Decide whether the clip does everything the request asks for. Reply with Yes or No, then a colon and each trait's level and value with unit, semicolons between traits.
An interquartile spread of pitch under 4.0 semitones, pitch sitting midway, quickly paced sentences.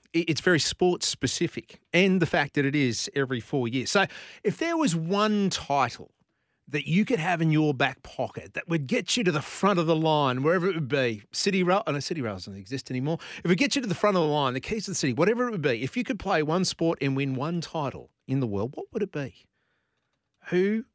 No: wide, 5.6 semitones; medium, 165 Hz; fast, 255 wpm